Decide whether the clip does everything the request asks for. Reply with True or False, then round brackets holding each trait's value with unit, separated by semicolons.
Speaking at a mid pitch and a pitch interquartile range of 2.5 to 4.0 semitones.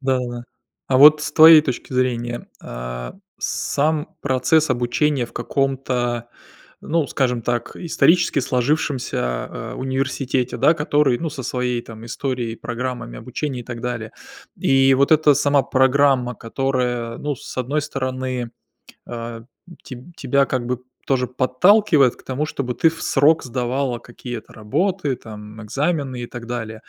False (130 Hz; 2.9 semitones)